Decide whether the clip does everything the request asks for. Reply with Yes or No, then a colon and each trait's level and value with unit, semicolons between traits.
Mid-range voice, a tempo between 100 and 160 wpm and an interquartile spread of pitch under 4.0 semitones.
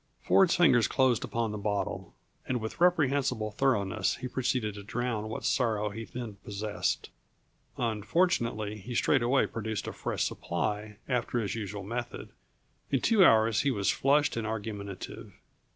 No: low, 115 Hz; average, 145 wpm; average, 3.4 semitones